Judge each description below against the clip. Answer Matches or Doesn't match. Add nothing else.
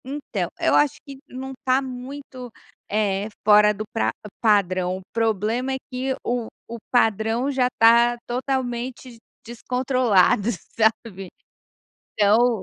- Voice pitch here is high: Matches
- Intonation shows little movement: Doesn't match